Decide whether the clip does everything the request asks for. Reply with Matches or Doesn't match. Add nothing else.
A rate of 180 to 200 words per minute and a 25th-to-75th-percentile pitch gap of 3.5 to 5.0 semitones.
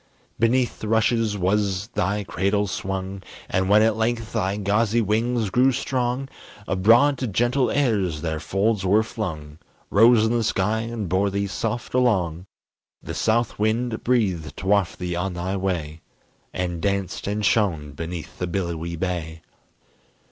Doesn't match